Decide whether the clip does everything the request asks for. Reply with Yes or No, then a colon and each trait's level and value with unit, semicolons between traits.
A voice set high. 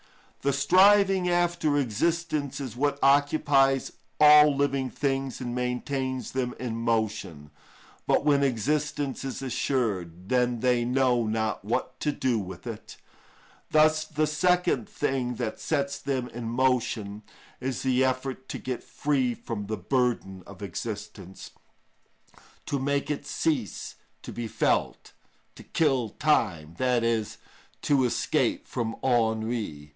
No: low, 130 Hz